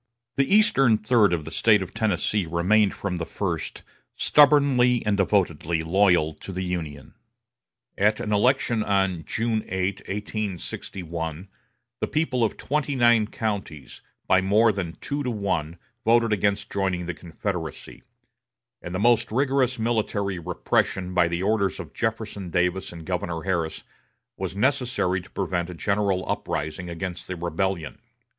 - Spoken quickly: No, average, 145 wpm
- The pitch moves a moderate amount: Yes, average, 4.1 semitones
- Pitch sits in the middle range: No, very low, 95 Hz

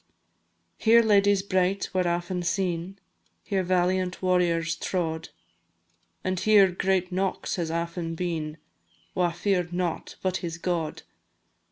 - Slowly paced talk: Yes, slow, 120 wpm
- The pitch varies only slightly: Yes, narrow, 1.7 semitones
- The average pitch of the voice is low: No, medium, 180 Hz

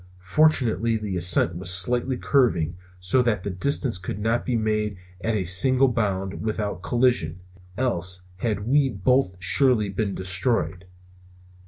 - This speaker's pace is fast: No, average, 140 wpm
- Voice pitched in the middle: No, low, 105 Hz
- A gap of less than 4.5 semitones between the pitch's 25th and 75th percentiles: No, average, 5.0 semitones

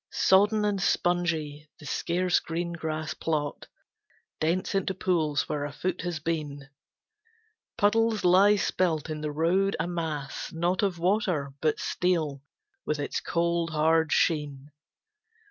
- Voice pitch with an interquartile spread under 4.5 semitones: Yes, average, 3.2 semitones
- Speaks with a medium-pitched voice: Yes, medium, 165 Hz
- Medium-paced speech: No, slow, 130 wpm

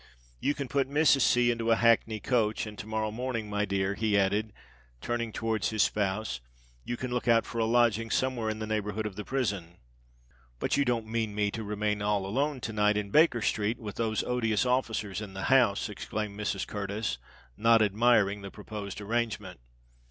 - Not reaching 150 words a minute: No, average, 190 wpm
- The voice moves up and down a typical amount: No, narrow, 2.3 semitones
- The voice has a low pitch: Yes, low, 110 Hz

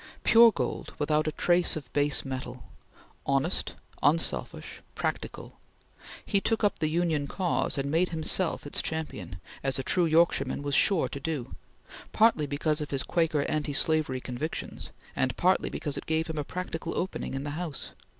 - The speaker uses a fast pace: No, average, 165 wpm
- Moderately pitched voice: Yes, medium, 155 Hz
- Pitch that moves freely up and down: No, average, 3.4 semitones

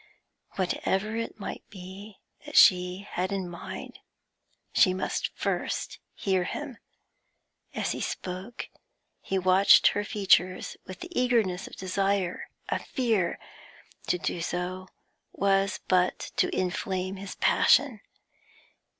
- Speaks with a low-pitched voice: No, high, 190 Hz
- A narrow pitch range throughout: Yes, narrow, 1.8 semitones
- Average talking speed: No, slow, 115 wpm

